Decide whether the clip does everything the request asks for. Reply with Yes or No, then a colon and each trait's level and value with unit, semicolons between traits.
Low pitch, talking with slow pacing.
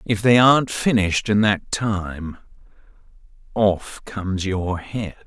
Yes: low, 100 Hz; slow, 125 wpm